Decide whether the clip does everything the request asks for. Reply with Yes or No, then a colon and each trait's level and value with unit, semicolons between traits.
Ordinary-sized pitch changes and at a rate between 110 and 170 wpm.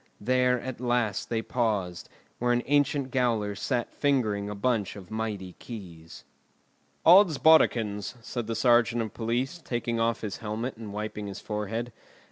Yes: average, 3.1 semitones; average, 145 wpm